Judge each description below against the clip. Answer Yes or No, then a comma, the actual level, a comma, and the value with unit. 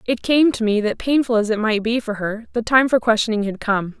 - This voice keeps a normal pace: No, fast, 270 wpm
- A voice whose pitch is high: Yes, high, 225 Hz